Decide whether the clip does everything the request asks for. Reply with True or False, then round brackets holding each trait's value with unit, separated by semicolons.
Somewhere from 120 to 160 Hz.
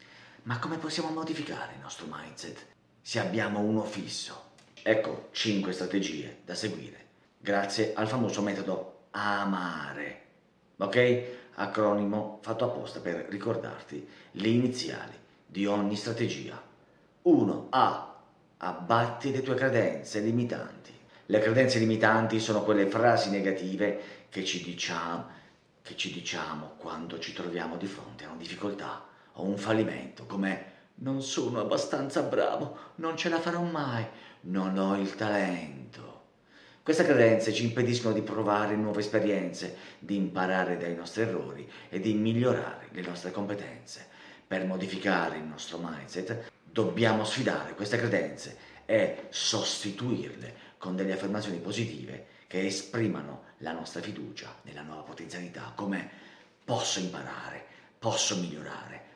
False (105 Hz)